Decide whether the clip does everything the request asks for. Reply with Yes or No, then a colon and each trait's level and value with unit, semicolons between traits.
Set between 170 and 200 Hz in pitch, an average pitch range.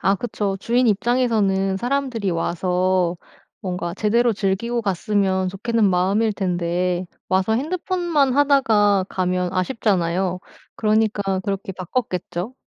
Yes: high, 195 Hz; average, 4.0 semitones